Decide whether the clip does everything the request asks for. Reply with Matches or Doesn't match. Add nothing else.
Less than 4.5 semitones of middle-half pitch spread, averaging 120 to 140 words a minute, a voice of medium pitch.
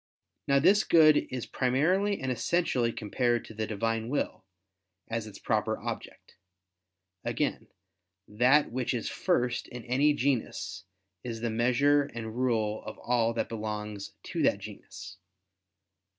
Doesn't match